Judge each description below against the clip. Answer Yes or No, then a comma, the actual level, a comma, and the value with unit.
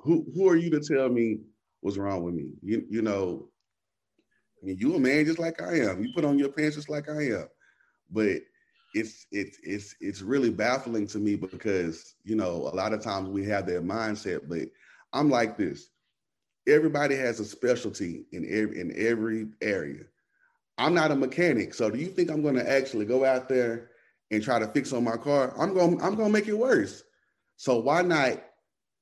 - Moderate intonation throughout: No, wide, 6.7 semitones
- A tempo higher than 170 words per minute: Yes, fast, 205 wpm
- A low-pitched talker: Yes, low, 130 Hz